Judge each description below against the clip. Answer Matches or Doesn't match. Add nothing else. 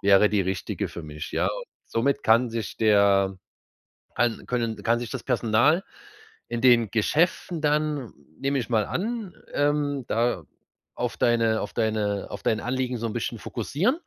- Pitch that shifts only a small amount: Doesn't match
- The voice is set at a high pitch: Doesn't match